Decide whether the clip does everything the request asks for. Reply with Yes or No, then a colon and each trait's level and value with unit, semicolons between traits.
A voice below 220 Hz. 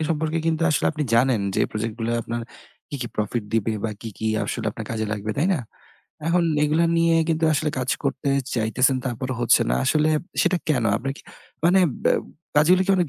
Yes: low, 135 Hz